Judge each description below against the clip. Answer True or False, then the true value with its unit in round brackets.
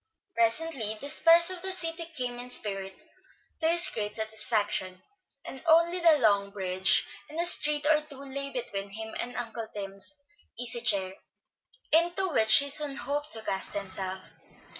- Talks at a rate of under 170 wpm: True (160 wpm)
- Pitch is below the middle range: False (245 Hz)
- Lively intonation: True (7.0 semitones)